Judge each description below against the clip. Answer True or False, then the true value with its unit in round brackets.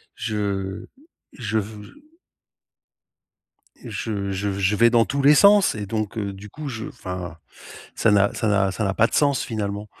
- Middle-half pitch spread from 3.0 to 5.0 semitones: False (2.6 semitones)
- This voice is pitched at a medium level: False (105 Hz)